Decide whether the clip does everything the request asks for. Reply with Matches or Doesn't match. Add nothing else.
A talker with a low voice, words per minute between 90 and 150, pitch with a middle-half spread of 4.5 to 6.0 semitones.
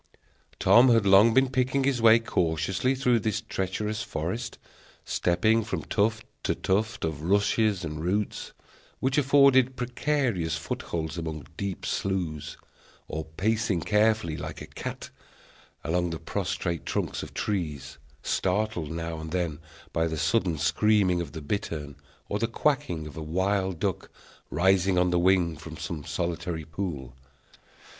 Matches